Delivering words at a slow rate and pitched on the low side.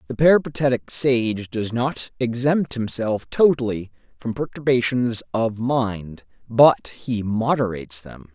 Yes: slow, 115 wpm; low, 115 Hz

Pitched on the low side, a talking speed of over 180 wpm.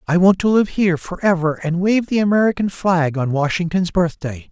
No: medium, 175 Hz; average, 200 wpm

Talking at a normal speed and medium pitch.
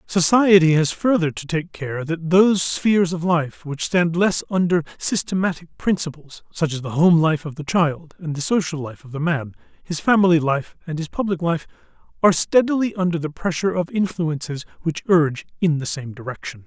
Yes: average, 185 wpm; medium, 165 Hz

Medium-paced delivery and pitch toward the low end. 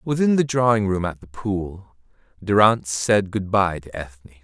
Yes: average, 175 wpm; low, 100 Hz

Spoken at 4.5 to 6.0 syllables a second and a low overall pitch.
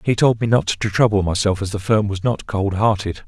Yes: 5.4 syllables/s; low, 105 Hz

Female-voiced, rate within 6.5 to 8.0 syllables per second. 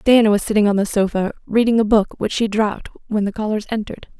Yes: female; 6.7 syllables/s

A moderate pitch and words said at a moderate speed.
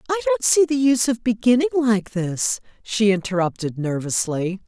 No: high, 230 Hz; average, 155 wpm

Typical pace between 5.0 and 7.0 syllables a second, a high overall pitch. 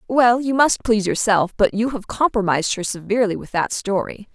Yes: 5.6 syllables/s; high, 215 Hz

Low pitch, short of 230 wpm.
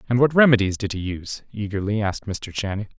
Yes: low, 105 Hz; average, 200 wpm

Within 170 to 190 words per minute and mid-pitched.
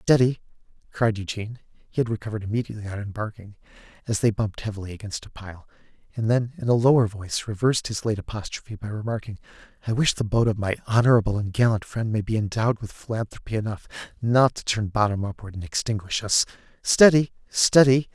No: average, 180 wpm; low, 110 Hz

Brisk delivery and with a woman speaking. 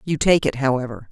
Yes: fast, 215 wpm; female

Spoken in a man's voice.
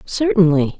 No: female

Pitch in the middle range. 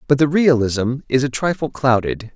No: low, 130 Hz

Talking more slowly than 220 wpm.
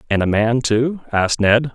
Yes: fast, 205 wpm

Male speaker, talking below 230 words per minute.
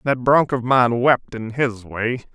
Yes: male; fast, 205 wpm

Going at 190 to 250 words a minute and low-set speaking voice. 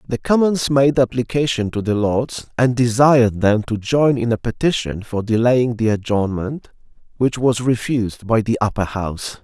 No: average, 165 wpm; low, 115 Hz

